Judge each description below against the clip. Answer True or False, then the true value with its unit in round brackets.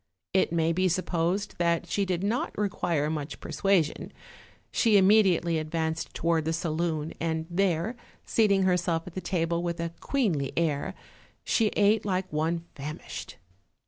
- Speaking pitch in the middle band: True (170 Hz)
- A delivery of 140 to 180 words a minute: True (145 wpm)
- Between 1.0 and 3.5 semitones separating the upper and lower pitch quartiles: True (3.0 semitones)